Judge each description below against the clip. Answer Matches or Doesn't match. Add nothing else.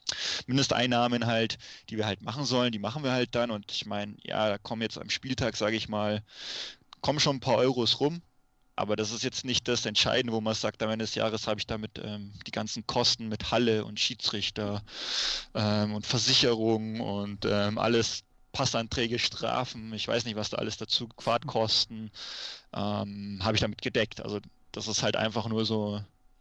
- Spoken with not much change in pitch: Matches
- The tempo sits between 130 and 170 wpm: Doesn't match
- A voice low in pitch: Matches